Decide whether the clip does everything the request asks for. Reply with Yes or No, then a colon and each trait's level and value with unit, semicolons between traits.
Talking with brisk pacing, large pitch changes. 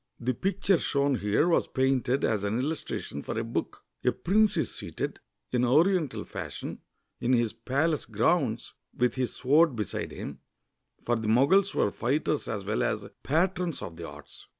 No: average, 165 wpm; wide, 6.0 semitones